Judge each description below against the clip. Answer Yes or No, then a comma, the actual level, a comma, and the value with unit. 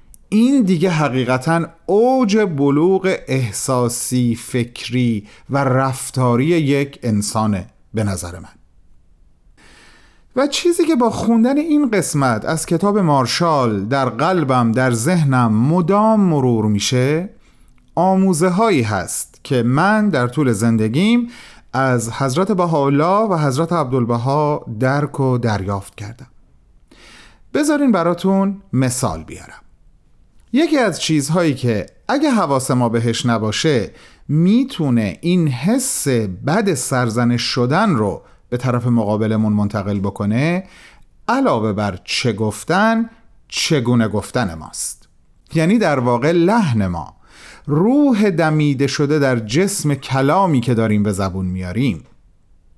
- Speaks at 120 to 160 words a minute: No, average, 110 wpm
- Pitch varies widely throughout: Yes, wide, 7.5 semitones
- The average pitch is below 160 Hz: Yes, low, 135 Hz